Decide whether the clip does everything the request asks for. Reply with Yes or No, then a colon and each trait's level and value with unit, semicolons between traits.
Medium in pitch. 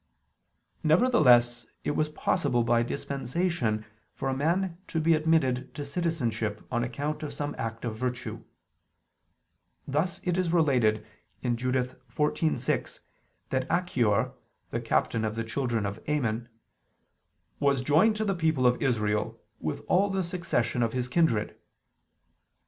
No: low, 130 Hz